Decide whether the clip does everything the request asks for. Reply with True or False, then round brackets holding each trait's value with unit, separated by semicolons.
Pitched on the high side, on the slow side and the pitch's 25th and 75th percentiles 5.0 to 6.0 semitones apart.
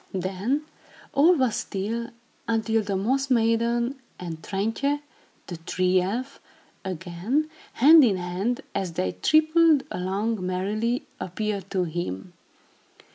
True (215 Hz; 115 wpm; 5.6 semitones)